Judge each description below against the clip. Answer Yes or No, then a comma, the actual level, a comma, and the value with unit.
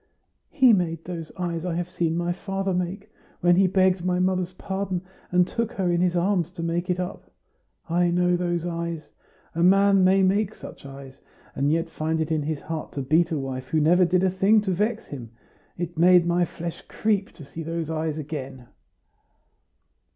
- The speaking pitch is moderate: Yes, medium, 175 Hz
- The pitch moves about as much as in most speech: No, narrow, 2.3 semitones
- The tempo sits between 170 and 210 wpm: Yes, average, 195 wpm